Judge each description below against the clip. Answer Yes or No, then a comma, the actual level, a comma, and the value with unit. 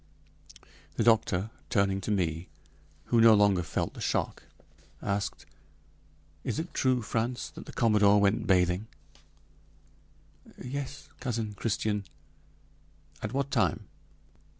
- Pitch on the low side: Yes, low, 105 Hz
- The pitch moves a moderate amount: Yes, average, 3.2 semitones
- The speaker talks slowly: Yes, slow, 115 wpm